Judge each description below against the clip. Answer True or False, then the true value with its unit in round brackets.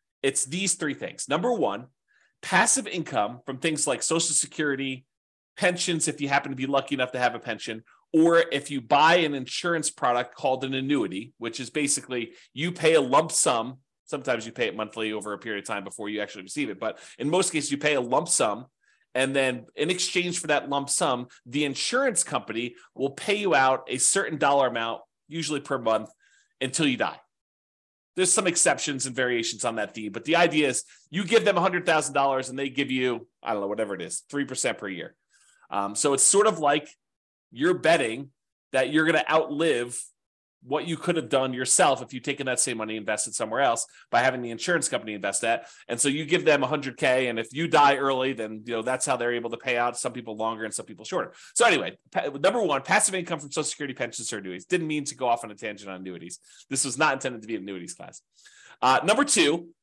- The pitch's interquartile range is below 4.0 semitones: False (4.9 semitones)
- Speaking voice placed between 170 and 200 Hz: False (135 Hz)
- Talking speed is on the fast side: True (220 wpm)